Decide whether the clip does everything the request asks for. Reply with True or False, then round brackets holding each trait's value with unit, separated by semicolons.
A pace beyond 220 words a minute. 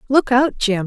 False (210 wpm)